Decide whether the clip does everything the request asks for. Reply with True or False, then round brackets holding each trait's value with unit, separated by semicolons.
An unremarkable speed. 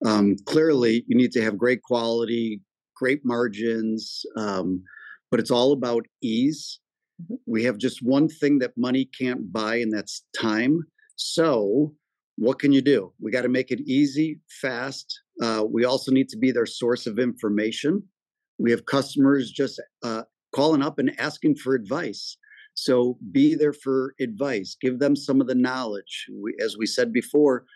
True (165 wpm)